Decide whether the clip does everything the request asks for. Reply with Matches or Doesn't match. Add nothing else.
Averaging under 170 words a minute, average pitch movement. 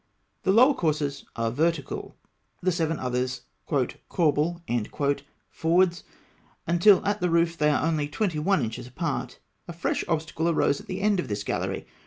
Matches